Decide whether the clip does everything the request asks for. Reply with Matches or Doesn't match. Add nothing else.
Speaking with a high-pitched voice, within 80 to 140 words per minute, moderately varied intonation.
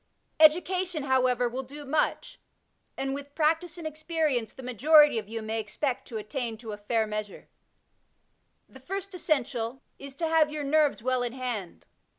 Doesn't match